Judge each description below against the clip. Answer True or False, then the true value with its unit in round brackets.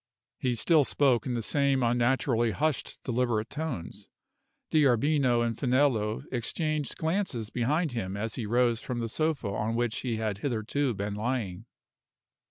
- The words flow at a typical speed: True (145 wpm)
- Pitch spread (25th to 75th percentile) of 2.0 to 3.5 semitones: False (3.9 semitones)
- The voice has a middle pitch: False (120 Hz)